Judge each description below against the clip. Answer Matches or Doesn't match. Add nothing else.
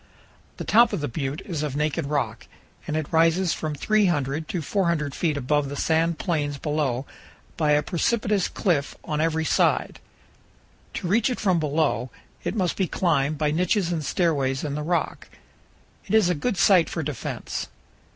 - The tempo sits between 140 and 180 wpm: Matches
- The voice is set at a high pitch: Doesn't match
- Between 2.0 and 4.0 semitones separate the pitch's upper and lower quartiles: Matches